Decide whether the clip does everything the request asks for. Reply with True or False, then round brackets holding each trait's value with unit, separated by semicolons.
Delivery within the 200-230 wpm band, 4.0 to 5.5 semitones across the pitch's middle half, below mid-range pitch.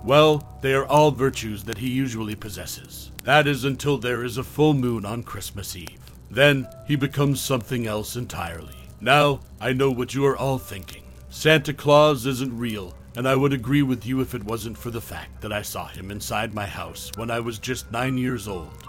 True (205 wpm; 4.5 semitones; 125 Hz)